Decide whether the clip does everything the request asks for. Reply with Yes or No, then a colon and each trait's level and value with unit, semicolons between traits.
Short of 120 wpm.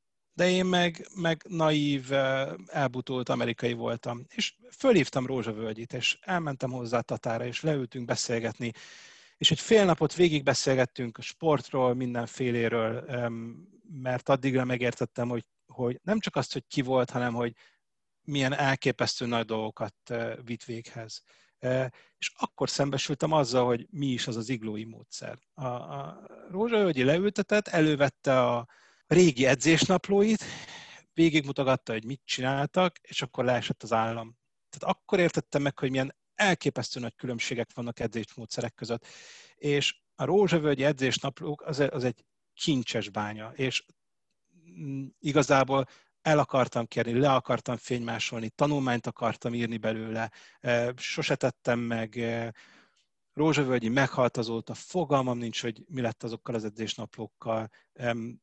No: average, 125 wpm